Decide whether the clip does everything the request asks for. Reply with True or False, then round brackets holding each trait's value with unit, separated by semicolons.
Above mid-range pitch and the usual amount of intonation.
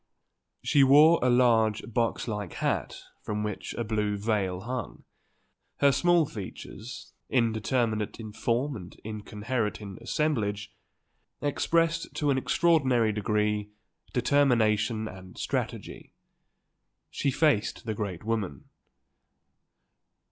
False (110 Hz; 3.9 semitones)